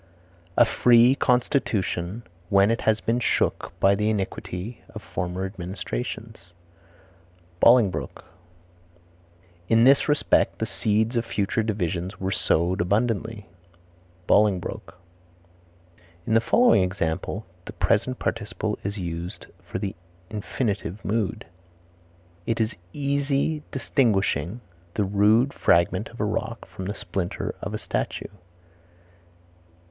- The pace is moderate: No, slow, 110 wpm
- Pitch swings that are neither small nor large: Yes, average, 3.6 semitones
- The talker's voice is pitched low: Yes, low, 105 Hz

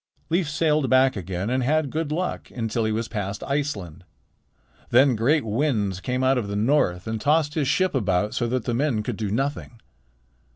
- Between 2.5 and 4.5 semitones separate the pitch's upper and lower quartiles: No, wide, 5.4 semitones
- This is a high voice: No, low, 125 Hz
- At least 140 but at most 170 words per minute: No, average, 190 wpm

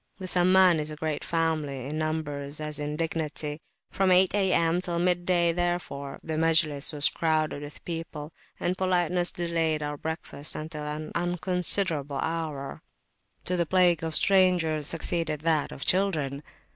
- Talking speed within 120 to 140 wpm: No, average, 150 wpm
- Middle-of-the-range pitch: Yes, medium, 160 Hz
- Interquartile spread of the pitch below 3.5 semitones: Yes, average, 2.7 semitones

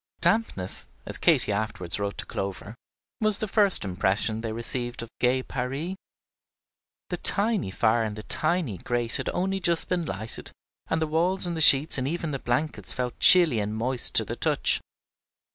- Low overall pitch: Yes, low, 125 Hz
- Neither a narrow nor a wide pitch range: No, wide, 7.7 semitones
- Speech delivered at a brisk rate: No, average, 175 wpm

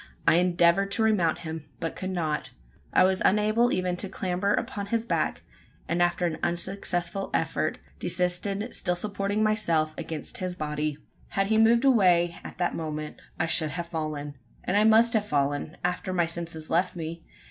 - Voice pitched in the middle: Yes, medium, 180 Hz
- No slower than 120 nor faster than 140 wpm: No, average, 170 wpm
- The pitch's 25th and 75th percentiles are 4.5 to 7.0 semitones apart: No, average, 3.5 semitones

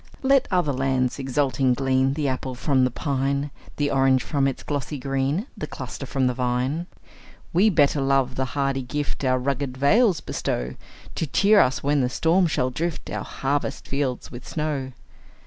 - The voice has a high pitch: No, low, 135 Hz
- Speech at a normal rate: Yes, average, 170 wpm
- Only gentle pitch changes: Yes, narrow, 2.2 semitones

